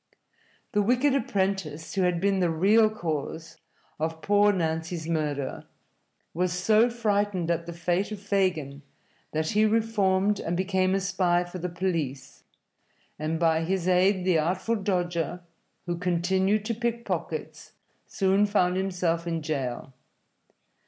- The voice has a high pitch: No, medium, 180 Hz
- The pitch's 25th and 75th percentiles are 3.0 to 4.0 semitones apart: Yes, average, 3.4 semitones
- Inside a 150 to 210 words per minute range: No, average, 140 wpm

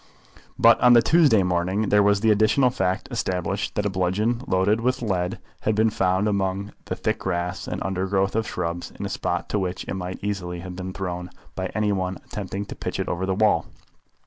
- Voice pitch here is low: Yes, very low, 95 Hz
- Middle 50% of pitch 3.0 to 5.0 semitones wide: No, narrow, 2.6 semitones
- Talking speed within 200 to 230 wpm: Yes, fast, 205 wpm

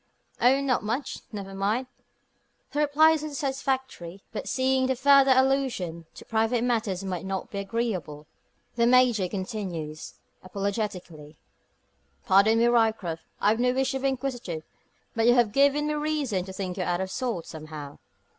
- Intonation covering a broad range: Yes, wide, 5.9 semitones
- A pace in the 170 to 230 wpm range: No, average, 155 wpm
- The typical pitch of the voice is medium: No, high, 225 Hz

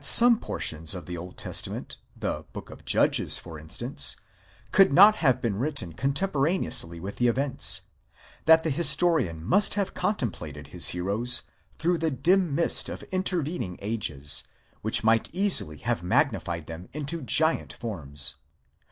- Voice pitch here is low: Yes, low, 125 Hz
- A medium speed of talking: Yes, average, 145 wpm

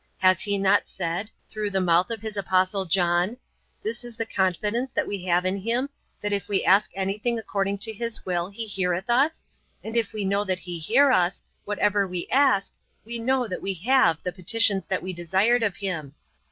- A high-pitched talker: Yes, high, 200 Hz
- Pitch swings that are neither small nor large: Yes, average, 3.5 semitones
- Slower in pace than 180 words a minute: No, average, 200 wpm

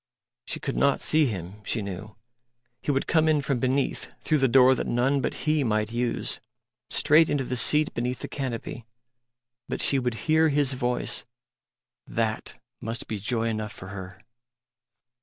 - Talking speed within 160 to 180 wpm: Yes, average, 165 wpm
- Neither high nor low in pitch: No, low, 125 Hz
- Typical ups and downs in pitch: Yes, average, 4.2 semitones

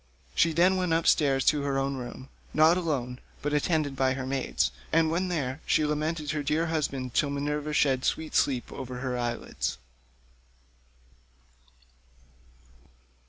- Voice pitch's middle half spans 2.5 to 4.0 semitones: Yes, average, 3.2 semitones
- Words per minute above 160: No, average, 140 wpm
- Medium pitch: Yes, medium, 145 Hz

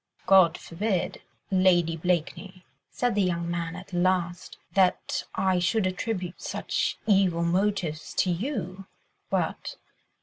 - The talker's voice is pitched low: No, medium, 185 Hz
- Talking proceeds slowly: Yes, slow, 115 wpm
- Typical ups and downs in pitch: No, narrow, 2.0 semitones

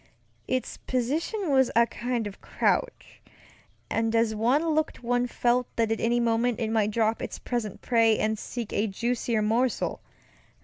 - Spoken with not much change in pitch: Yes, narrow, 1.9 semitones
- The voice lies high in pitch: Yes, high, 235 Hz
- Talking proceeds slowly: No, average, 160 wpm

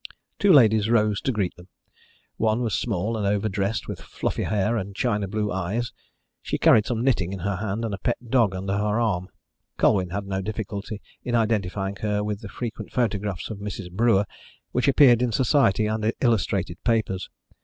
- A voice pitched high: No, low, 105 Hz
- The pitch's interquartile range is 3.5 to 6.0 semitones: No, average, 2.7 semitones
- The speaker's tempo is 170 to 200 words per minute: Yes, average, 180 wpm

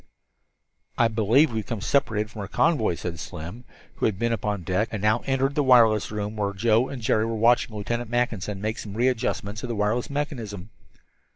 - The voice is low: Yes, low, 110 Hz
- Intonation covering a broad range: No, average, 2.7 semitones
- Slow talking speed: No, average, 190 wpm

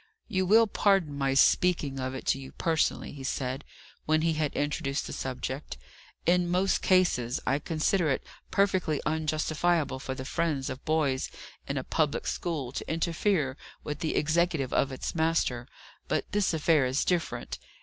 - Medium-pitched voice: Yes, medium, 155 Hz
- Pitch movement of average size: Yes, average, 4.1 semitones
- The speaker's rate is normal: Yes, average, 160 wpm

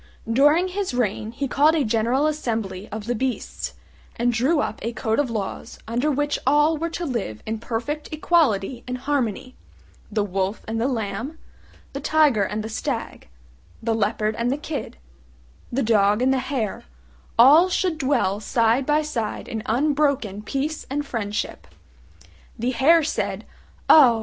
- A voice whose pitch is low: No, very high, 250 Hz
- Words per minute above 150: Yes, average, 160 wpm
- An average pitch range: Yes, average, 4.9 semitones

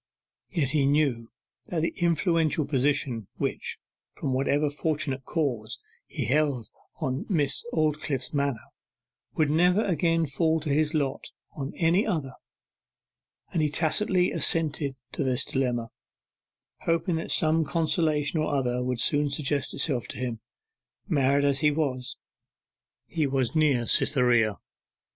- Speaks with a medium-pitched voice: Yes, medium, 145 Hz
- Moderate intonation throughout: Yes, average, 3.2 semitones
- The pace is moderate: No, slow, 130 wpm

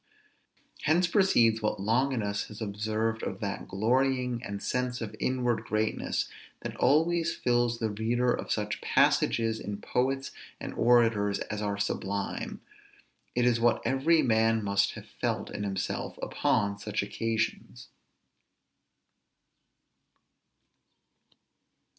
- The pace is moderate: No, slow, 115 wpm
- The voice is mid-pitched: No, low, 115 Hz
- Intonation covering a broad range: No, average, 3.2 semitones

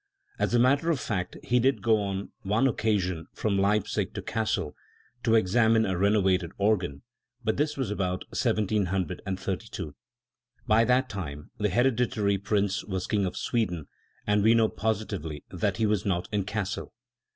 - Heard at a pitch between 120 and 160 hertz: No, low, 105 Hz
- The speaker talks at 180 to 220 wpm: No, average, 155 wpm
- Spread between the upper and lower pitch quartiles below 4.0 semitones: Yes, average, 3.1 semitones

